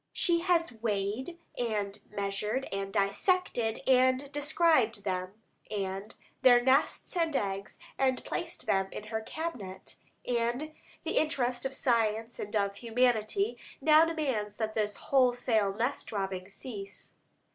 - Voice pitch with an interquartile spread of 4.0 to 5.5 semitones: Yes, average, 5.0 semitones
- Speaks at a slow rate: Yes, slow, 125 wpm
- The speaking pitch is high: Yes, high, 230 Hz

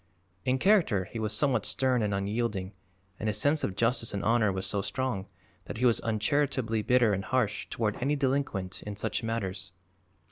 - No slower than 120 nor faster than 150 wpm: No, average, 180 wpm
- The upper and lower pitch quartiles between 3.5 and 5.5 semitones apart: Yes, average, 4.3 semitones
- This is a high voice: No, low, 110 Hz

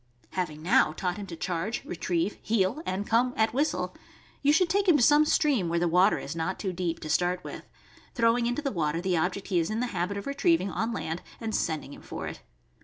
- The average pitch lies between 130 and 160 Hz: No, high, 195 Hz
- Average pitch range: No, wide, 5.9 semitones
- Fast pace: Yes, fast, 230 wpm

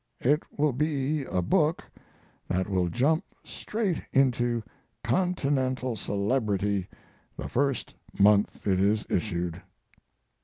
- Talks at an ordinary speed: No, slow, 105 wpm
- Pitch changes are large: Yes, wide, 6.4 semitones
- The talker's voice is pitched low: Yes, low, 120 Hz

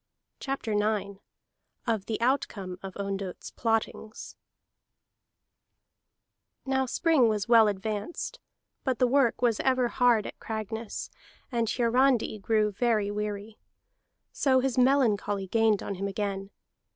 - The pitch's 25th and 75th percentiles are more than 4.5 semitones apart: No, average, 3.3 semitones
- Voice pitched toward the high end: Yes, high, 220 Hz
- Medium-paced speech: No, slow, 115 wpm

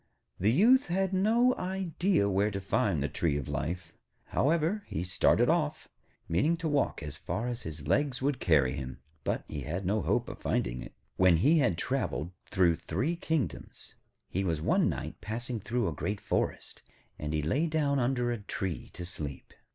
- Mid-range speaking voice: No, low, 105 Hz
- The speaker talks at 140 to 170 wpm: No, average, 180 wpm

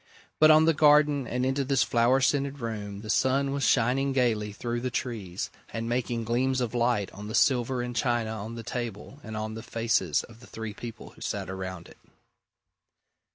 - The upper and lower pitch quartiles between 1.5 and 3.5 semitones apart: Yes, average, 3.1 semitones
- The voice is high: No, low, 120 Hz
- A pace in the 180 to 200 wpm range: Yes, average, 195 wpm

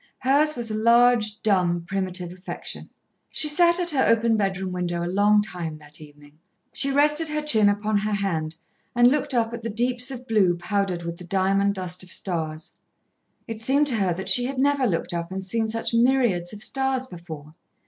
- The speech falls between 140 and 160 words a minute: No, average, 195 wpm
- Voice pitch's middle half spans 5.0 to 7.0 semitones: Yes, wide, 5.5 semitones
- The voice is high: Yes, high, 210 Hz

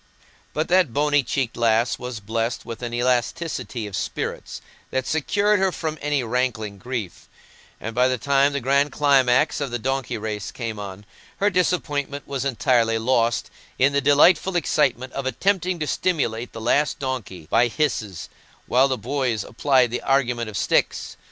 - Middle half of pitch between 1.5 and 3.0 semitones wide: No, average, 3.9 semitones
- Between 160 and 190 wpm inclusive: Yes, average, 165 wpm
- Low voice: Yes, low, 130 Hz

